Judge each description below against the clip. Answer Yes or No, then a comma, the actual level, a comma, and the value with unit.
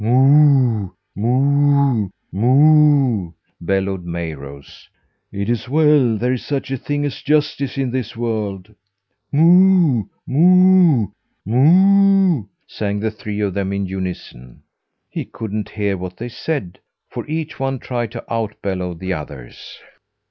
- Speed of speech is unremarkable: No, slow, 125 wpm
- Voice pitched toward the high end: No, low, 120 Hz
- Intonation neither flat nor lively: No, wide, 6.6 semitones